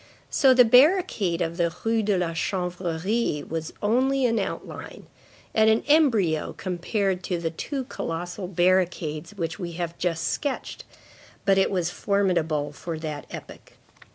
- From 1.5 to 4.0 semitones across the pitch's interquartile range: No, average, 4.7 semitones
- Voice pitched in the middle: Yes, medium, 180 Hz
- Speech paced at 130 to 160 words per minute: Yes, average, 145 wpm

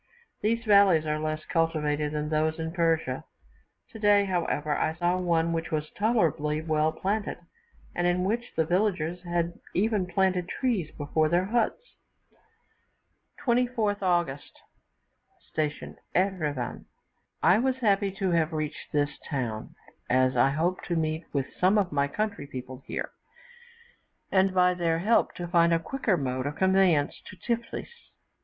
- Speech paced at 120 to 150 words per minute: Yes, average, 145 wpm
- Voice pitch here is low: No, medium, 170 Hz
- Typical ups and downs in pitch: Yes, average, 4.2 semitones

